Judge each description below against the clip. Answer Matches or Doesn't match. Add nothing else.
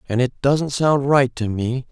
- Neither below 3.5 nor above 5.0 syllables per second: Matches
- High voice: Doesn't match